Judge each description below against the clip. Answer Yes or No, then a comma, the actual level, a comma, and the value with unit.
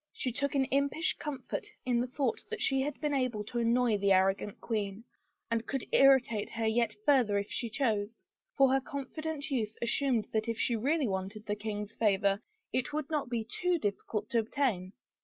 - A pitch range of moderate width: Yes, average, 4.3 semitones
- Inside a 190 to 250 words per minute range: Yes, average, 195 wpm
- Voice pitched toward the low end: No, high, 235 Hz